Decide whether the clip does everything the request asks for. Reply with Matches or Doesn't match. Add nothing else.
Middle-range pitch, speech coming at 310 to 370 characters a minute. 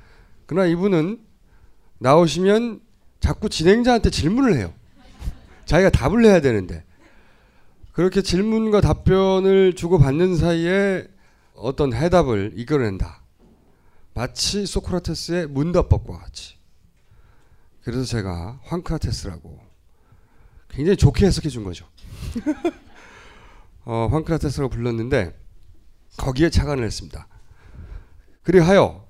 Doesn't match